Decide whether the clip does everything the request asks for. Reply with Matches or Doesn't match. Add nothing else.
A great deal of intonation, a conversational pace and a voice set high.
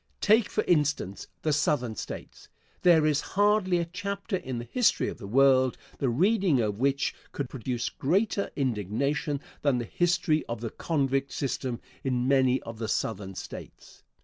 Doesn't match